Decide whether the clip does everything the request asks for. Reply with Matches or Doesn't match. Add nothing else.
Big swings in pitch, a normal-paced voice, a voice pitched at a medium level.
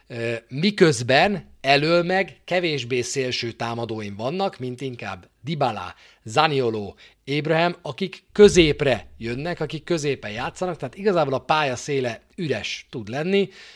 Matches